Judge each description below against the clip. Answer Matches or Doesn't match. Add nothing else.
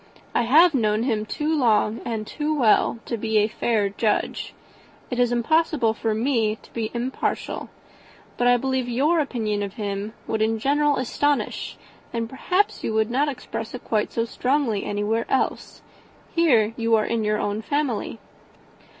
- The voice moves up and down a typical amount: Matches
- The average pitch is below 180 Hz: Doesn't match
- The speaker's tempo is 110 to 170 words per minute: Matches